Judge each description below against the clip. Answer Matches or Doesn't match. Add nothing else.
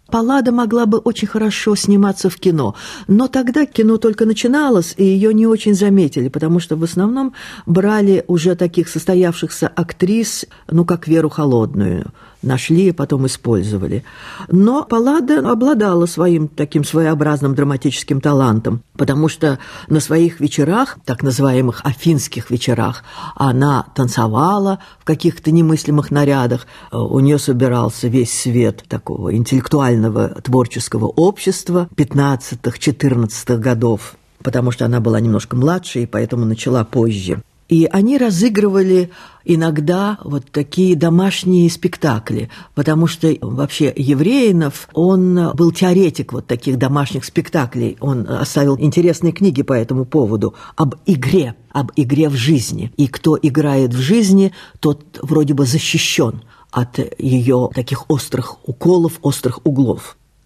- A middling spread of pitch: Doesn't match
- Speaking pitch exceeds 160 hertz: Doesn't match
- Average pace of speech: Matches